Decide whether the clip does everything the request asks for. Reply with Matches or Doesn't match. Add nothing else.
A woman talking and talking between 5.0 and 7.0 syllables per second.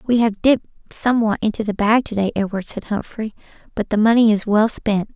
Matches